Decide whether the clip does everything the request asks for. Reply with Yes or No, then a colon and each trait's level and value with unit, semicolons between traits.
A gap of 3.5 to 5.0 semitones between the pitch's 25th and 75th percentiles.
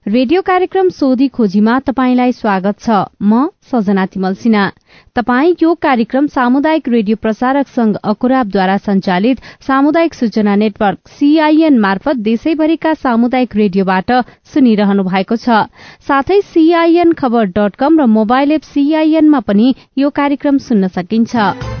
No: wide, 5.5 semitones